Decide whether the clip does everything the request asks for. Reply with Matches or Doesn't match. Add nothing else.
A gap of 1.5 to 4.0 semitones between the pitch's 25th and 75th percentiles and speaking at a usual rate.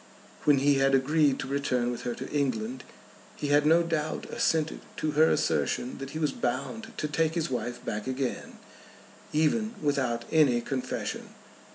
Matches